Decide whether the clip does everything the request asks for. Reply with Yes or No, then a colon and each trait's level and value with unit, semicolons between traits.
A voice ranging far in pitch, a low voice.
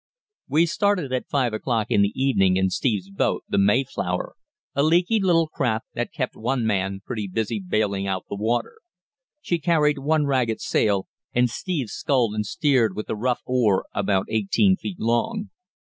Yes: wide, 6.2 semitones; low, 120 Hz